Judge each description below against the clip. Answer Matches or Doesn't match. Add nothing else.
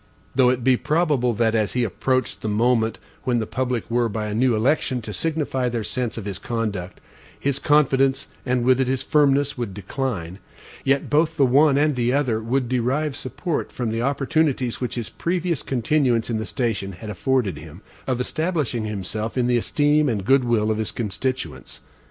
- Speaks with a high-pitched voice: Doesn't match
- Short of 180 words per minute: Doesn't match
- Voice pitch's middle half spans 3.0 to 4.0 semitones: Matches